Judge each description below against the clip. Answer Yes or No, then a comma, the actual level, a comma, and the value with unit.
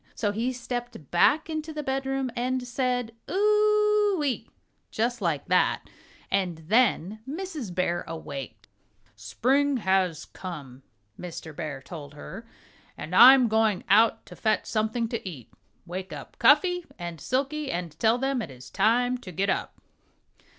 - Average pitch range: No, wide, 7.3 semitones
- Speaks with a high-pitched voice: Yes, high, 225 Hz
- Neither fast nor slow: Yes, average, 155 wpm